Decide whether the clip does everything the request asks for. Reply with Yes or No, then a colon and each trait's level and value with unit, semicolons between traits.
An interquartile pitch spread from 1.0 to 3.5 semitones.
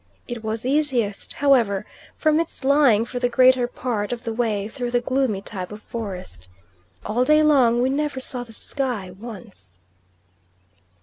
No: average, 3.9 semitones